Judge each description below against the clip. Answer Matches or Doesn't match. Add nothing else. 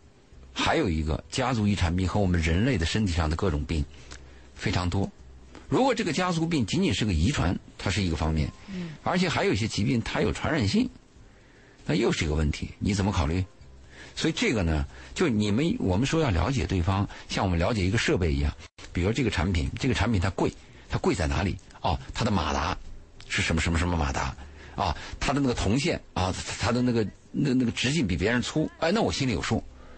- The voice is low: Matches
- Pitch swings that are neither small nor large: Doesn't match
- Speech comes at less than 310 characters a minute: Doesn't match